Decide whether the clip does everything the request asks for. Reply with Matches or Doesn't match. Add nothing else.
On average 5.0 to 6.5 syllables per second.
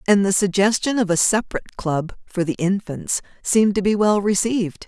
Matches